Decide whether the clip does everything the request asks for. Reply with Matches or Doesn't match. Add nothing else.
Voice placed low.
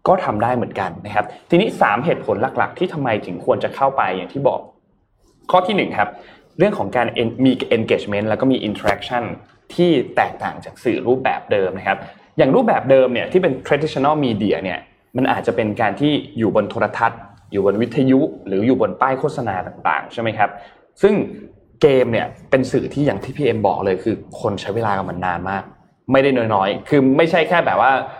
Matches